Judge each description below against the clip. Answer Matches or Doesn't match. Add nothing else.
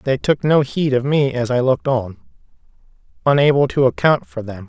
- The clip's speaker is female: Doesn't match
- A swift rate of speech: Doesn't match